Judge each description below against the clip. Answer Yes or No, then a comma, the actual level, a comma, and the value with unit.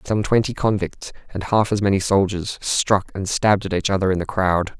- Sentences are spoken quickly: Yes, fast, 215 wpm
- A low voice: Yes, low, 100 Hz